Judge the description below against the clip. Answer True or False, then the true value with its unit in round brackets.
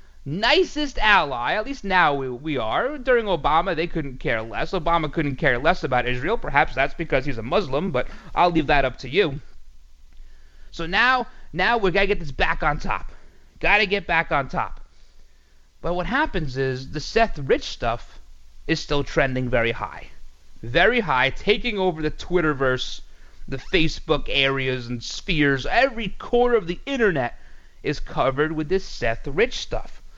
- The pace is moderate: True (170 wpm)